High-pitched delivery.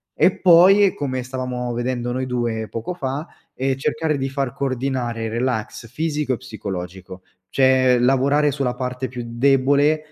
No: low, 130 Hz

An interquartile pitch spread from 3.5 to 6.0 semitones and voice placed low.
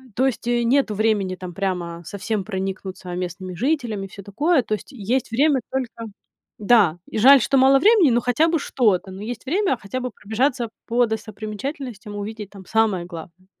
No: average, 5.0 semitones; high, 220 Hz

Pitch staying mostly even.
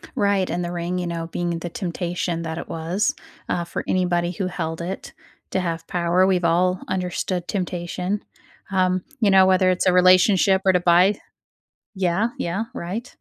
Yes: narrow, 1.5 semitones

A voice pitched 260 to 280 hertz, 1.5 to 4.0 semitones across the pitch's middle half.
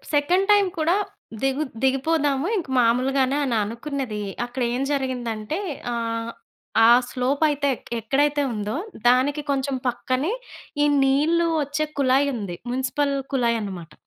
Yes: very high, 270 Hz; average, 3.4 semitones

